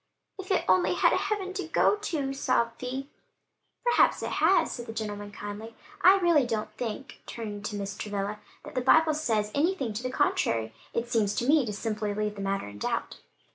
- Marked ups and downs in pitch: Yes, wide, 5.9 semitones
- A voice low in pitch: No, high, 230 Hz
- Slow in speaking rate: No, average, 200 wpm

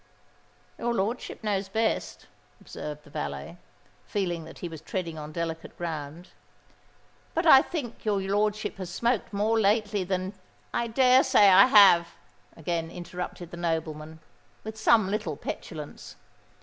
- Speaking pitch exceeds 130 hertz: Yes, high, 190 Hz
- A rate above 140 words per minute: No, slow, 135 wpm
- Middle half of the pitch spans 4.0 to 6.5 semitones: Yes, average, 4.6 semitones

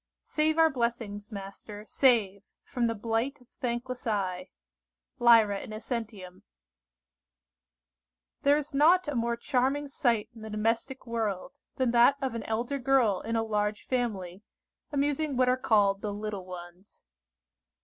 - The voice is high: Yes, high, 230 Hz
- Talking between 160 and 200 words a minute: No, average, 140 wpm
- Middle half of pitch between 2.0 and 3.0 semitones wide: No, average, 3.9 semitones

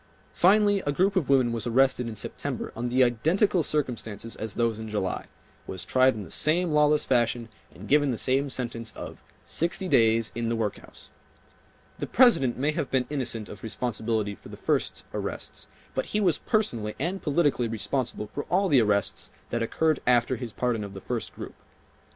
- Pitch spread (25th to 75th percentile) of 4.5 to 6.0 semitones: Yes, average, 4.8 semitones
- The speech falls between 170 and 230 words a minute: Yes, average, 180 wpm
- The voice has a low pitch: Yes, low, 125 Hz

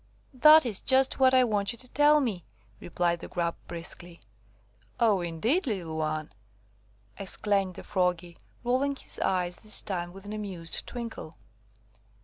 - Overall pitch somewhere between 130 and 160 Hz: No, high, 195 Hz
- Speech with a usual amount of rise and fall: No, wide, 6.0 semitones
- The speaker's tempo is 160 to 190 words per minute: No, average, 145 wpm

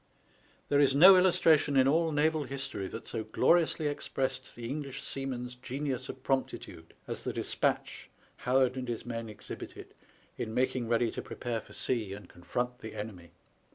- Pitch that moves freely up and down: No, average, 3.4 semitones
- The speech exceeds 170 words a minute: No, average, 165 wpm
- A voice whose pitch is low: Yes, low, 130 Hz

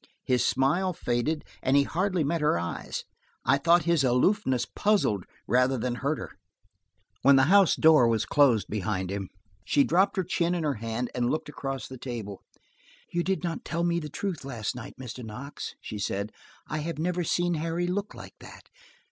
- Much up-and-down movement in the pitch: Yes, wide, 5.9 semitones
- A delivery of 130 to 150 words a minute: No, average, 190 wpm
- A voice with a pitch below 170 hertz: Yes, medium, 140 Hz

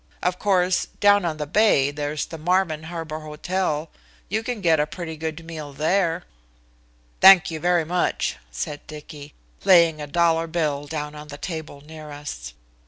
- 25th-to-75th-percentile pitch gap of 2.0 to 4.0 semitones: Yes, average, 2.9 semitones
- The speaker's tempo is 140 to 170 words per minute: Yes, average, 165 wpm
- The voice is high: No, medium, 160 Hz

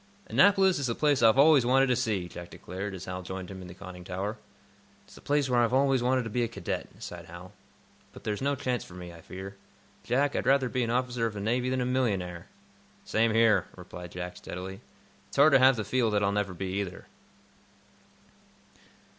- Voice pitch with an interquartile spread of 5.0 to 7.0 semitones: Yes, wide, 5.6 semitones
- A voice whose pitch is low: Yes, low, 110 Hz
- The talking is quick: Yes, fast, 215 wpm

